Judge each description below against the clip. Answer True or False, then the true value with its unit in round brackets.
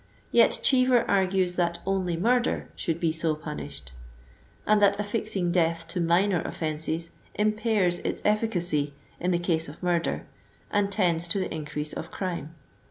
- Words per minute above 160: False (150 wpm)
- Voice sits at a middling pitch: True (175 Hz)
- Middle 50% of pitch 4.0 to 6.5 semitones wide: False (3.5 semitones)